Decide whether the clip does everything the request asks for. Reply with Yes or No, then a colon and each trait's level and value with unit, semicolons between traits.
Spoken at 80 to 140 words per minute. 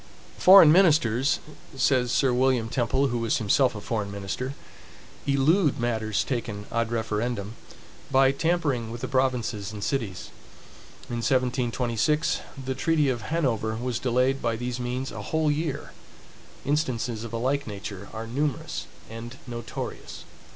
Yes: slow, 135 wpm